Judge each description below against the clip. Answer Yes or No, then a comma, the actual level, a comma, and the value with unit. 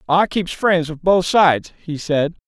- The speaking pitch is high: No, medium, 170 Hz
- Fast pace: No, average, 195 wpm